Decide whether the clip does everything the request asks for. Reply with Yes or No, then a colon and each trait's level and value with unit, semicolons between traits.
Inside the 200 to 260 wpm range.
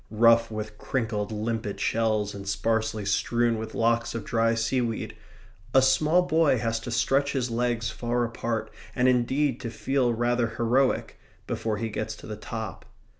No: average, 160 wpm